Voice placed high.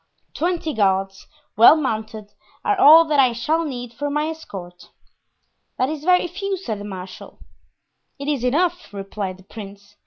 Yes: very high, 250 Hz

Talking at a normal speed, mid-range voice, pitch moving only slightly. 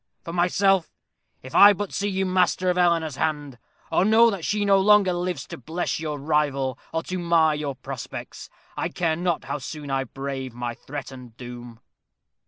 No: average, 180 wpm; medium, 160 Hz; average, 5.2 semitones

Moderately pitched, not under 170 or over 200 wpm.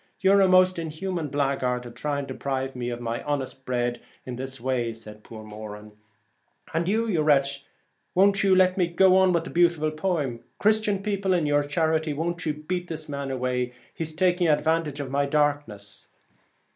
Yes: medium, 150 Hz; average, 180 wpm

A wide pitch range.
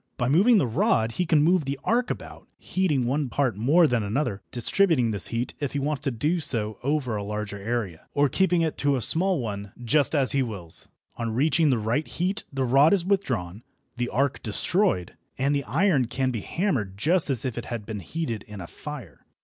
Yes: wide, 5.9 semitones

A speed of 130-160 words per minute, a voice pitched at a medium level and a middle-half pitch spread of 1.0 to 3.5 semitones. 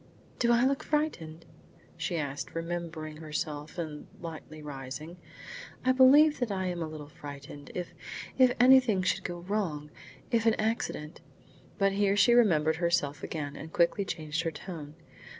No: average, 155 wpm; medium, 170 Hz; average, 5.3 semitones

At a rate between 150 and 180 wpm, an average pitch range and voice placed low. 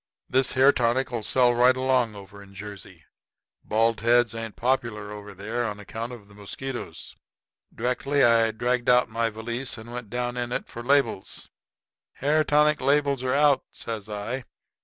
Yes: average, 160 wpm; average, 3.0 semitones; low, 120 Hz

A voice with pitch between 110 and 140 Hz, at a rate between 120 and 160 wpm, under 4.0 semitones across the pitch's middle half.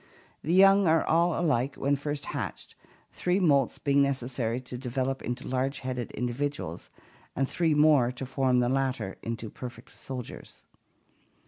Yes: low, 135 Hz; average, 145 wpm; average, 2.9 semitones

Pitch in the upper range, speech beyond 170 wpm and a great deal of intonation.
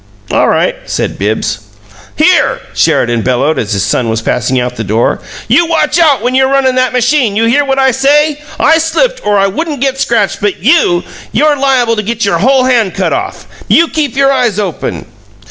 Yes: very high, 250 Hz; average, 200 wpm; wide, 6.9 semitones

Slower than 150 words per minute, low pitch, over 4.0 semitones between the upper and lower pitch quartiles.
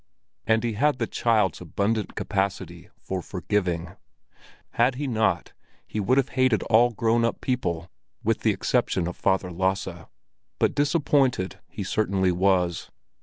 Yes: average, 140 wpm; low, 105 Hz; average, 4.4 semitones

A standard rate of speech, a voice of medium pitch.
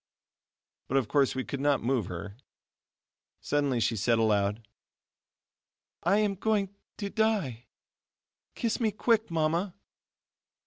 No: slow, 120 wpm; medium, 145 Hz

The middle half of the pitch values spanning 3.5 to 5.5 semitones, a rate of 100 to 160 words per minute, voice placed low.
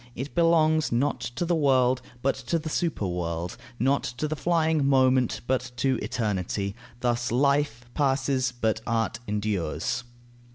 Yes: average, 4.4 semitones; slow, 135 wpm; low, 130 Hz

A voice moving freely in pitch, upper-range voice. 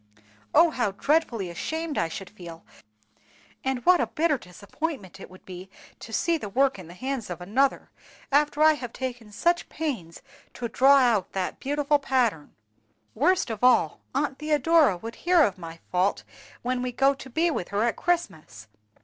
Yes: wide, 7.3 semitones; very high, 250 Hz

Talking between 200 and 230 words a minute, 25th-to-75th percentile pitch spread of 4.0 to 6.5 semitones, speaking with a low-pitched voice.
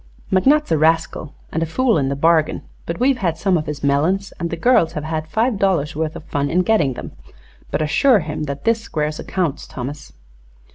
No: fast, 205 wpm; average, 4.4 semitones; medium, 160 Hz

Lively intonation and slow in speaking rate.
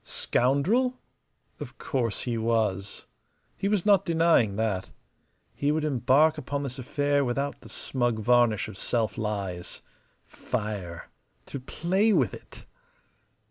Yes: wide, 5.8 semitones; slow, 125 wpm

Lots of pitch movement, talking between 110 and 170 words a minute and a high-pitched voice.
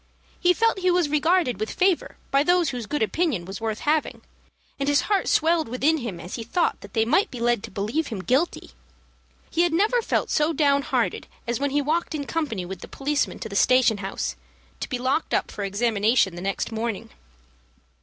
No: wide, 6.6 semitones; fast, 205 wpm; very high, 270 Hz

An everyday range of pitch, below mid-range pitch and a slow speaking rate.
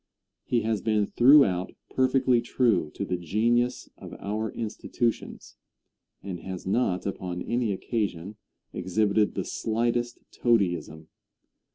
Yes: average, 4.2 semitones; low, 110 Hz; slow, 110 wpm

